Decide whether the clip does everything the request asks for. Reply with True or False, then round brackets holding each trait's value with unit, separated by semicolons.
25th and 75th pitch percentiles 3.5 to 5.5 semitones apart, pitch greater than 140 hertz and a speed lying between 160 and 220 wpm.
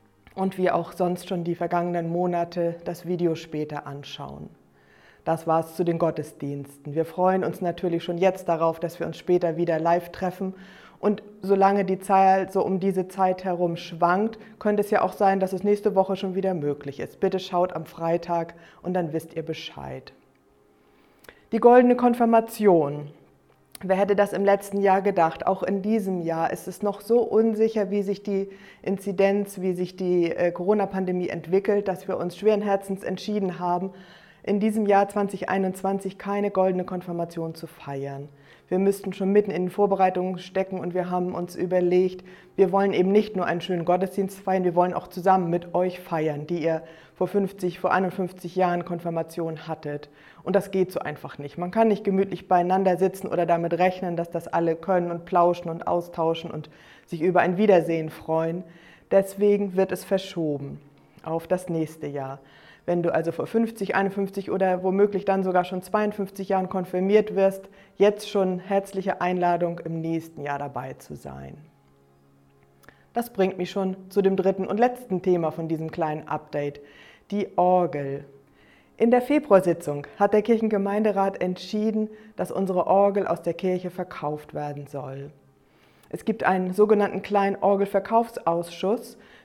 False (2.8 semitones; 185 Hz; 165 wpm)